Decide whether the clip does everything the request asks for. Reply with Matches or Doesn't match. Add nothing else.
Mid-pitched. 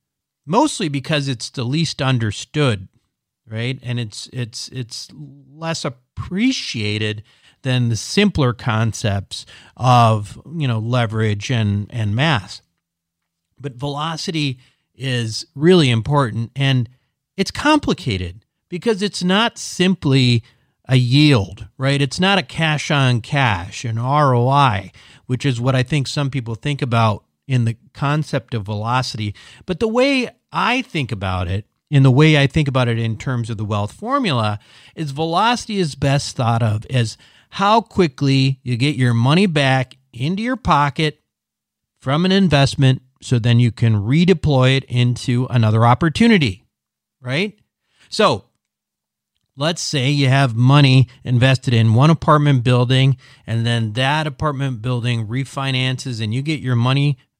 Doesn't match